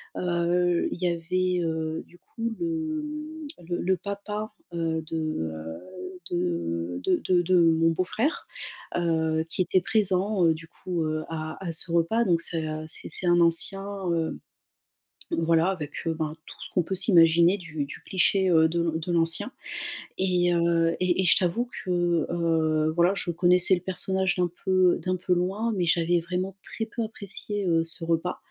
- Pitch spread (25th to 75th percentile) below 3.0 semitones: Yes, narrow, 2.4 semitones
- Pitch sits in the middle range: Yes, medium, 175 Hz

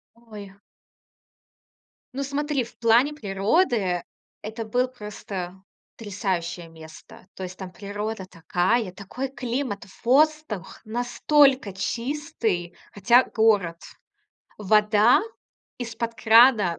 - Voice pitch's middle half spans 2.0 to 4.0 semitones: No, average, 4.5 semitones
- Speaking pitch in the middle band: No, high, 220 Hz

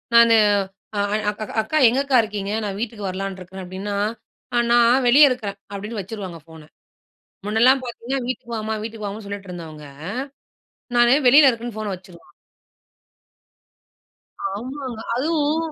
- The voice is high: Yes, high, 220 Hz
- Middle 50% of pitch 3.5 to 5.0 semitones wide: Yes, average, 3.9 semitones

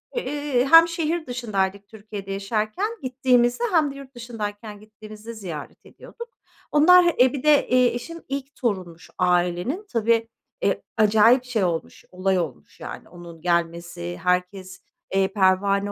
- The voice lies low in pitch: No, high, 215 Hz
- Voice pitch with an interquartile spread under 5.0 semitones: No, wide, 5.6 semitones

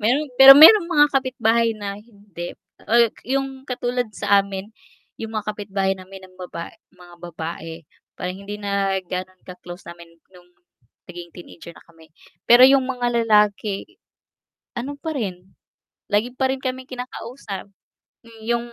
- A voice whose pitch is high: Yes, high, 210 Hz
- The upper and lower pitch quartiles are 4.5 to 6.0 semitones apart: Yes, average, 5.1 semitones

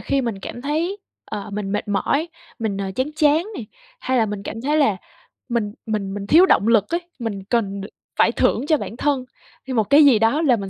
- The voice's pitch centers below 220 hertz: No, high, 230 Hz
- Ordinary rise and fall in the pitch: No, wide, 5.9 semitones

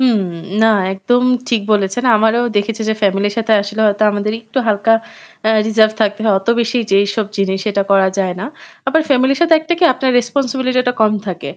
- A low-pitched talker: No, high, 220 Hz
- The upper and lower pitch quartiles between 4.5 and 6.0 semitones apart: No, average, 3.4 semitones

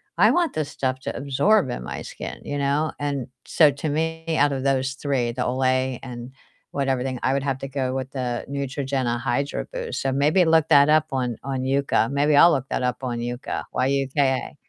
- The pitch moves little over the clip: Yes, narrow, 1.9 semitones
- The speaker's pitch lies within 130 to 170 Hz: Yes, low, 135 Hz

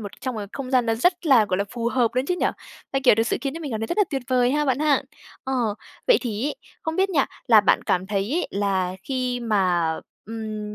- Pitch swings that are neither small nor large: Yes, average, 4.6 semitones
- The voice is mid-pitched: No, high, 245 Hz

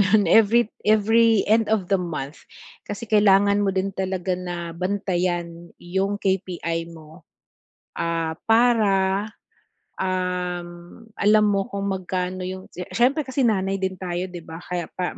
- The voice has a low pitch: No, high, 190 Hz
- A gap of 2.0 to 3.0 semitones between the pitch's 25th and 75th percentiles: Yes, narrow, 2.5 semitones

